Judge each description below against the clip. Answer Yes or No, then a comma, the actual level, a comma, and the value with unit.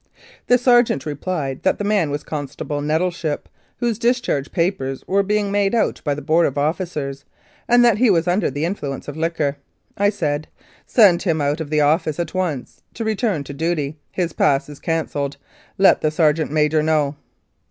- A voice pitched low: No, medium, 160 Hz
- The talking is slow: No, average, 180 wpm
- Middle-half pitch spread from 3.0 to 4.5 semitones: No, average, 5.1 semitones